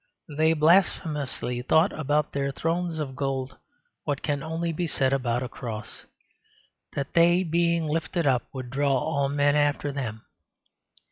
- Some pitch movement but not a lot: Yes, average, 3.3 semitones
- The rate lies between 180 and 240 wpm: No, average, 145 wpm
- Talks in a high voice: No, medium, 145 Hz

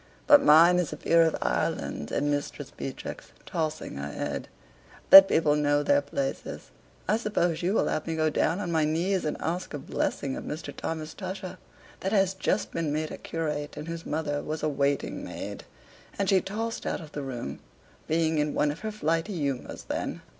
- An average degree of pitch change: Yes, average, 3.6 semitones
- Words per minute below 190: No, average, 195 wpm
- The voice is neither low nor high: Yes, medium, 160 Hz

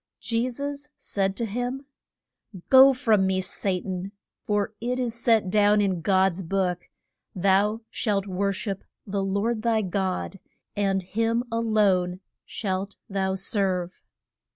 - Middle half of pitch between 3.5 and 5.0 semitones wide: No, average, 3.1 semitones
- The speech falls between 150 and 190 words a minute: No, slow, 135 wpm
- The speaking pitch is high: Yes, high, 200 Hz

